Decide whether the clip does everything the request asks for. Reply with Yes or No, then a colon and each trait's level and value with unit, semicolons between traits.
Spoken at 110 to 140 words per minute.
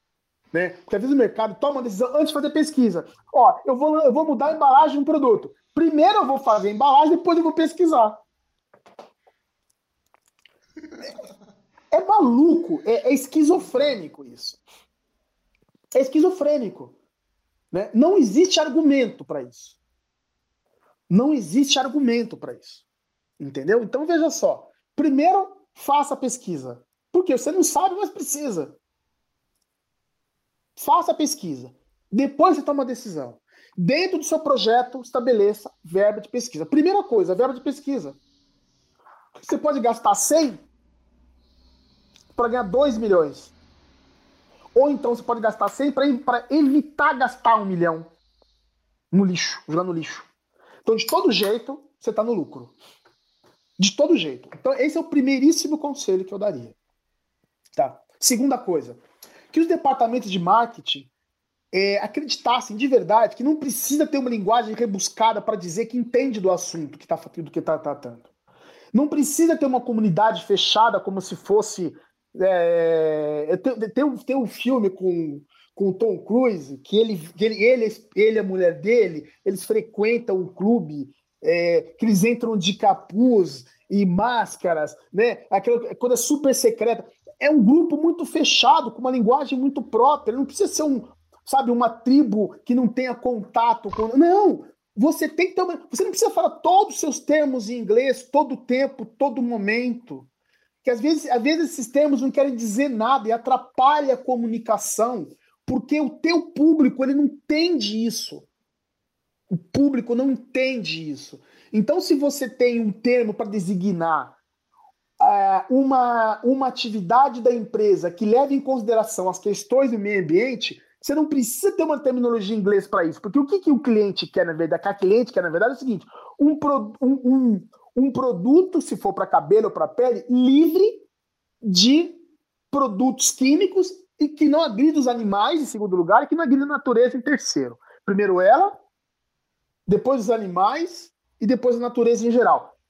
No: average, 160 wpm